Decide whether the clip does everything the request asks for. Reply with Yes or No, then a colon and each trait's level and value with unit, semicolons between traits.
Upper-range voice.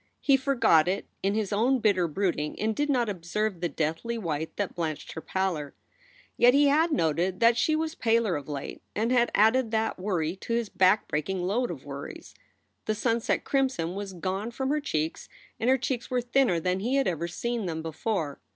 Yes: high, 205 Hz